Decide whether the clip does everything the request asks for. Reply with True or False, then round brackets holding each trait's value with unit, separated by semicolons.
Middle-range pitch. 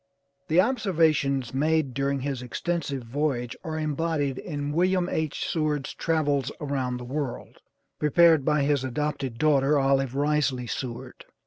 True (145 Hz)